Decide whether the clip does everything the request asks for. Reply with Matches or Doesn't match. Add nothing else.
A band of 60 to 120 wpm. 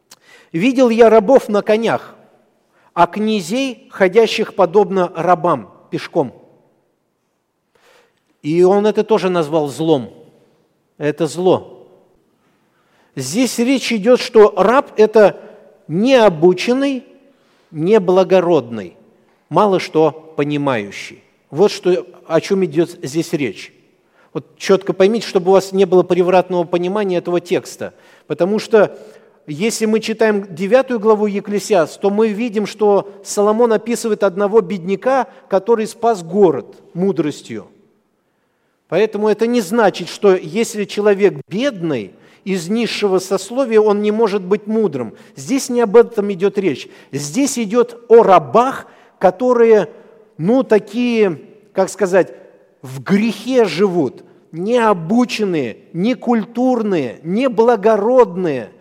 Matches